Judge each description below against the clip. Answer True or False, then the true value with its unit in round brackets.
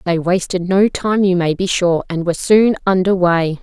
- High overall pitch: False (180 Hz)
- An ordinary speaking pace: False (215 wpm)